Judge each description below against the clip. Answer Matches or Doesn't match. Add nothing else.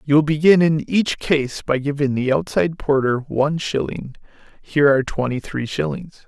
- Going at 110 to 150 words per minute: Doesn't match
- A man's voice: Matches